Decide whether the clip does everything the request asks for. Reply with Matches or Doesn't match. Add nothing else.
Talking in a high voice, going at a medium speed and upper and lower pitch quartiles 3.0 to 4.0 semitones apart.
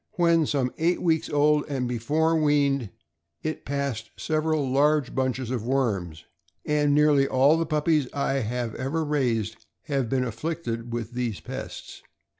Doesn't match